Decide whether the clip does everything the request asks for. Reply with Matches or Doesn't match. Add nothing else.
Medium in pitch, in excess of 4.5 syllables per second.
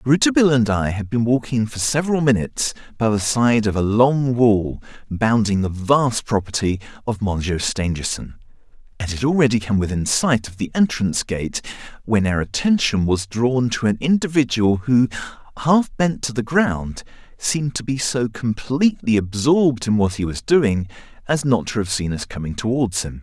Doesn't match